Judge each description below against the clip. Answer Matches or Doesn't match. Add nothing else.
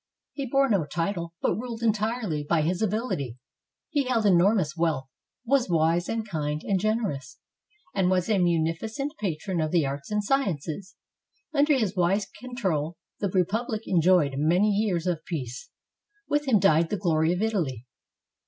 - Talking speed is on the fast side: Doesn't match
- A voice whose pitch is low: Doesn't match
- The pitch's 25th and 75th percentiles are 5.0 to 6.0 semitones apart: Matches